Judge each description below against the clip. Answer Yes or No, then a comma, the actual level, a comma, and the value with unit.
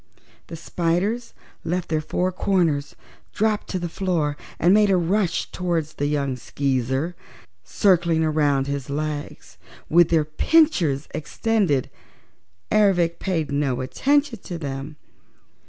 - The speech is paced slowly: Yes, slow, 120 wpm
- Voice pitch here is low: No, medium, 165 Hz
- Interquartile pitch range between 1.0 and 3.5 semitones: No, average, 4.3 semitones